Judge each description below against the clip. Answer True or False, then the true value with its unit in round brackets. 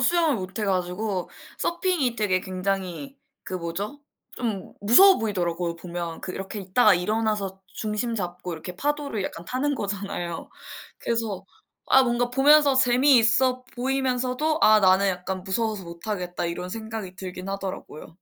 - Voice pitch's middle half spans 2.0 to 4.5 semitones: False (5.4 semitones)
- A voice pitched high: True (205 Hz)